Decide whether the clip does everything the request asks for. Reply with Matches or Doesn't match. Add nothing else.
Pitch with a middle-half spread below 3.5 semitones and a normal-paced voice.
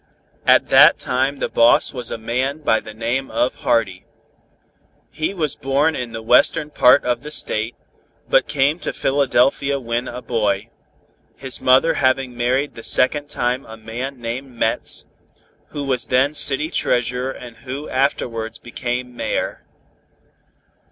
Matches